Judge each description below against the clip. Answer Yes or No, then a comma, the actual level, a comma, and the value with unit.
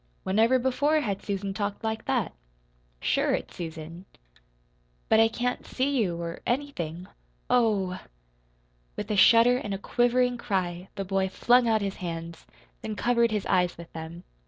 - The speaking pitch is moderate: No, high, 205 Hz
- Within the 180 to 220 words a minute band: No, average, 160 wpm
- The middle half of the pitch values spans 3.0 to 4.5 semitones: No, average, 5.0 semitones